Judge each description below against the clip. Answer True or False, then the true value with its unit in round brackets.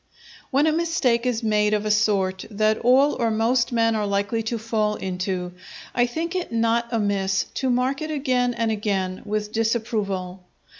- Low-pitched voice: False (225 Hz)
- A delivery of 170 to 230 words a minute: True (180 wpm)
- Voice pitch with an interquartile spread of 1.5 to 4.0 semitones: True (3.1 semitones)